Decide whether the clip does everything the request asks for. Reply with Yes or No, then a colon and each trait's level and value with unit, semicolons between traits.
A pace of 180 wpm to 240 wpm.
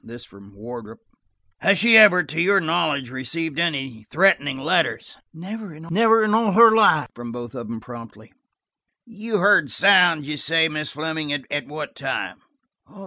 No: average, 150 wpm